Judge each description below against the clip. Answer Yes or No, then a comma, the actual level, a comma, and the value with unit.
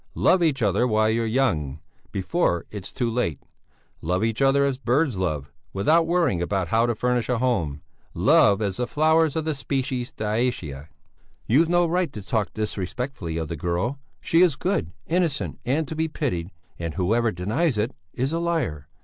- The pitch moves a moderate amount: No, wide, 7.7 semitones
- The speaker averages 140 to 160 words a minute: No, average, 175 wpm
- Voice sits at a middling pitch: No, low, 120 Hz